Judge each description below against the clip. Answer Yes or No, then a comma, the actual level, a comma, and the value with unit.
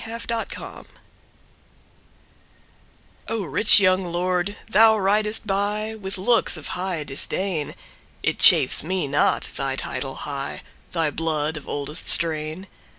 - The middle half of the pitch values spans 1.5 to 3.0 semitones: No, average, 5.3 semitones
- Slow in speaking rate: Yes, slow, 100 wpm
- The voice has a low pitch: No, medium, 185 Hz